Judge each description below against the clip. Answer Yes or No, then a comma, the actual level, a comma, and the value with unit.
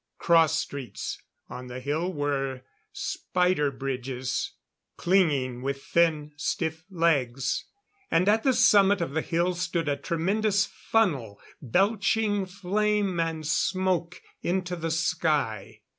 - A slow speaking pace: Yes, slow, 115 wpm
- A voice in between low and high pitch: Yes, medium, 165 Hz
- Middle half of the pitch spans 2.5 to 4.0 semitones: No, average, 5.3 semitones